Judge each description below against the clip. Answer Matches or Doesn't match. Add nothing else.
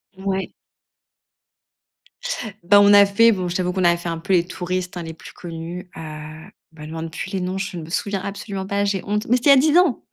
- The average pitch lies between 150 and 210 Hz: Matches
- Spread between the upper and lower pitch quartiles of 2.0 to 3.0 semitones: Matches